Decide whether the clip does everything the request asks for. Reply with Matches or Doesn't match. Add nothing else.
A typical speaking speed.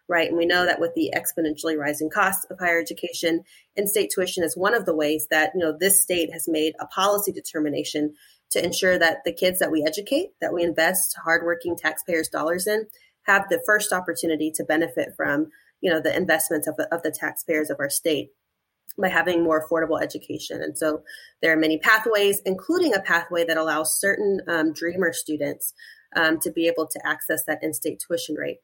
Matches